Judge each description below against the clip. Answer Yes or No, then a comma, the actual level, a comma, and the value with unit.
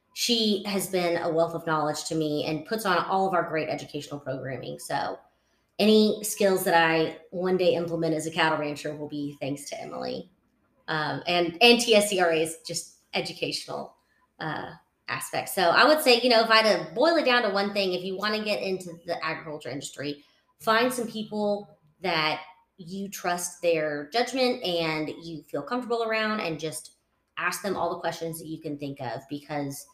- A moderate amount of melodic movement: Yes, average, 4.7 semitones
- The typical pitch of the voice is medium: Yes, medium, 170 Hz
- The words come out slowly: No, average, 190 wpm